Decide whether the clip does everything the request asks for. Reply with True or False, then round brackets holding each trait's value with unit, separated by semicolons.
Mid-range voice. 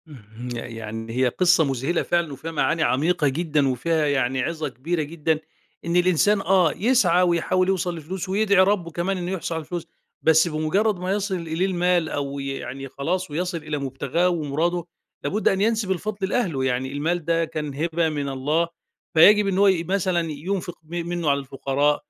True (165 Hz)